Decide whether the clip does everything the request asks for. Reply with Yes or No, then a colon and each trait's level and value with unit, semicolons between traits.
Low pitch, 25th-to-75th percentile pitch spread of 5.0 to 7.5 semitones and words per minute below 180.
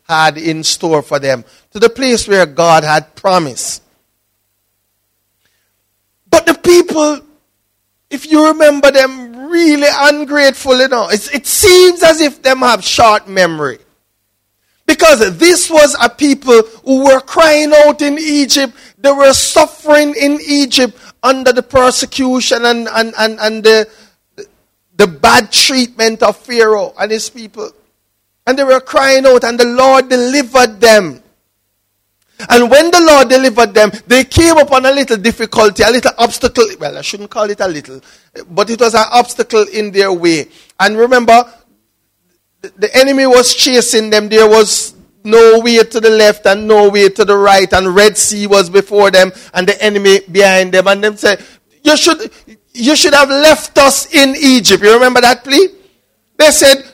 No: high, 235 Hz; wide, 5.4 semitones; average, 160 wpm